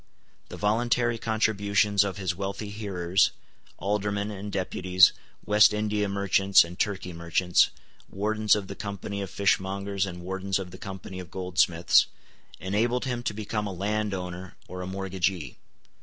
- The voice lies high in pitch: No, low, 100 Hz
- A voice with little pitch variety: Yes, narrow, 2.1 semitones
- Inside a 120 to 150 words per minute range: Yes, average, 140 wpm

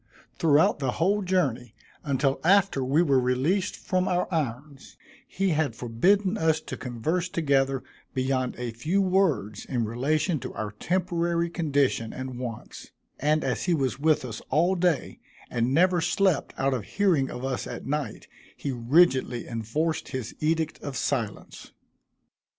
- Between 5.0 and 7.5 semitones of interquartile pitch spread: Yes, average, 5.3 semitones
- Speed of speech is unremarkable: Yes, average, 150 wpm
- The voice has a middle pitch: Yes, medium, 145 Hz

